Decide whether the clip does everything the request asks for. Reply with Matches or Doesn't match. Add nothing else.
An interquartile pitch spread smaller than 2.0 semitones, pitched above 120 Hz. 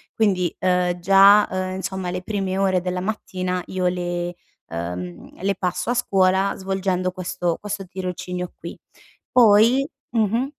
Matches